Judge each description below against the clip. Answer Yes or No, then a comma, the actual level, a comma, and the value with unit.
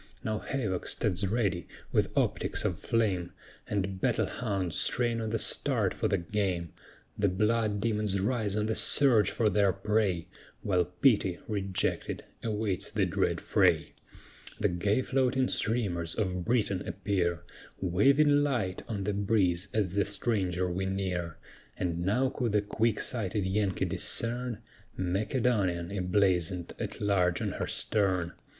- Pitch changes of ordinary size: Yes, average, 3.3 semitones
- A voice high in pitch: No, low, 100 Hz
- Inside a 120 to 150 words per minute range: Yes, average, 140 wpm